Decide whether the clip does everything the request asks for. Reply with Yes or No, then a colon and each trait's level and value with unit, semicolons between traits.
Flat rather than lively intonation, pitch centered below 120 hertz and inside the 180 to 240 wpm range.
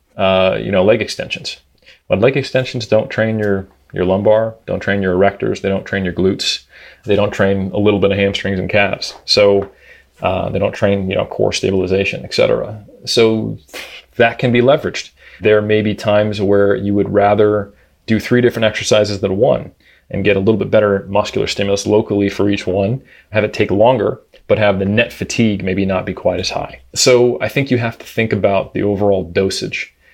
Yes: narrow, 1.9 semitones; low, 100 Hz; average, 195 wpm